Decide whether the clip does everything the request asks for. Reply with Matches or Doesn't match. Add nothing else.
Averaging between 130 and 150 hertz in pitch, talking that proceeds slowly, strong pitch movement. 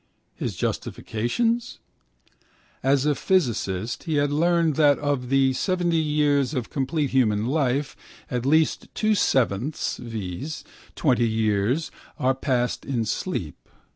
Doesn't match